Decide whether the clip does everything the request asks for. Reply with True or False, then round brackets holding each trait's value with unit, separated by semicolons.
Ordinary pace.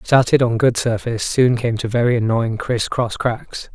True (190 wpm)